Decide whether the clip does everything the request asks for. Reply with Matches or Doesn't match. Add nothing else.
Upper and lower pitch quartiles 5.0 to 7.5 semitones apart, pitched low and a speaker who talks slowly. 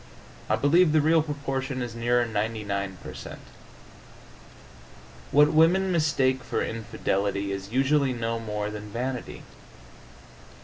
Matches